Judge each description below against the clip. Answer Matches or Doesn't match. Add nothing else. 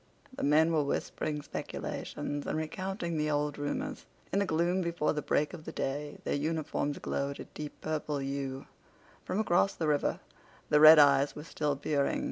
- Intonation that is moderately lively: Doesn't match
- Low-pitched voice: Doesn't match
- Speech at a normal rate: Matches